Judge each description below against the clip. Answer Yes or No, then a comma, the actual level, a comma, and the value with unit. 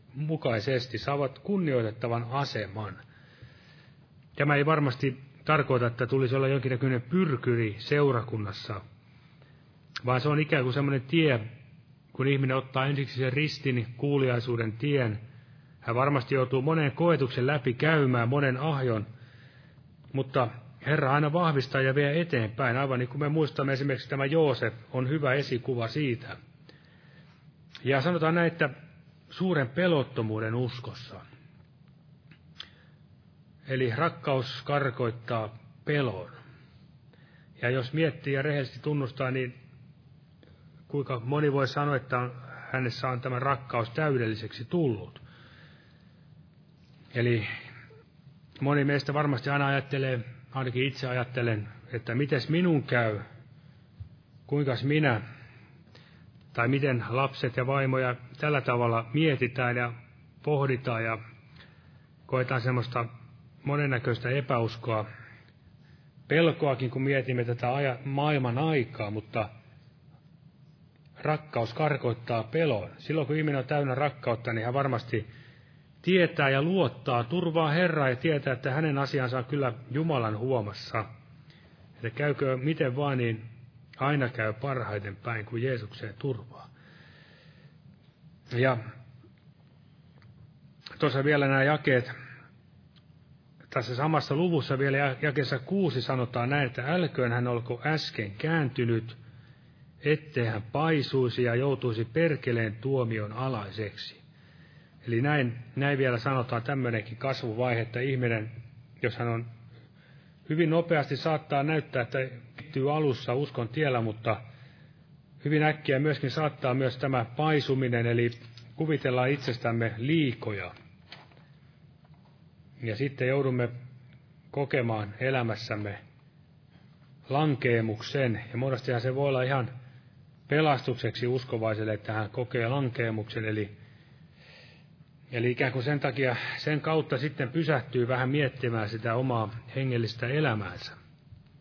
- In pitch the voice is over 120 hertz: Yes, low, 135 Hz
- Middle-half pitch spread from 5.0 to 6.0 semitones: No, average, 3.4 semitones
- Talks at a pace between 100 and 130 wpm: Yes, average, 105 wpm